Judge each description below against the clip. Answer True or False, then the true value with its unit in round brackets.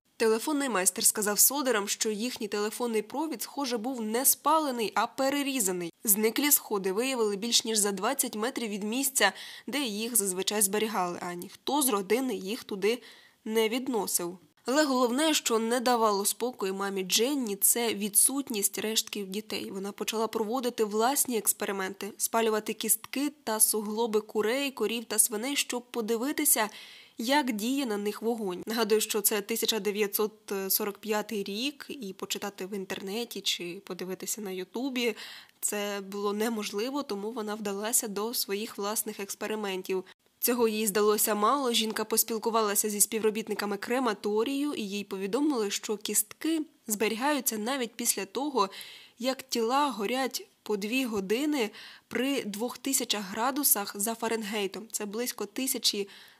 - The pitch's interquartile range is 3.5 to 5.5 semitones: False (2.9 semitones)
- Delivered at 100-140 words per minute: True (130 wpm)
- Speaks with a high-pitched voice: True (220 Hz)